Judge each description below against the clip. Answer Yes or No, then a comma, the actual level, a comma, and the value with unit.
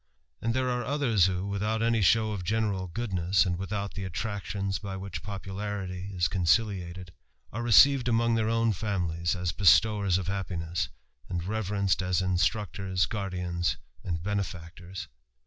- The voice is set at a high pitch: No, very low, 95 Hz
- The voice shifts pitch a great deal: No, average, 3.1 semitones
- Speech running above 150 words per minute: No, average, 145 wpm